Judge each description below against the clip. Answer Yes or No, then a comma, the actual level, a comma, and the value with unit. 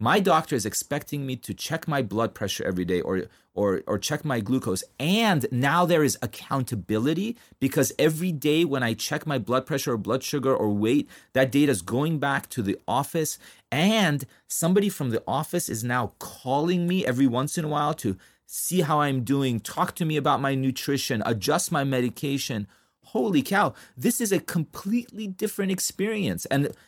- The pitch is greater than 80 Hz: Yes, medium, 140 Hz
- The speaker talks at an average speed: Yes, average, 185 wpm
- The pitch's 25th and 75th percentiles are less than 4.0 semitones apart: No, average, 5.1 semitones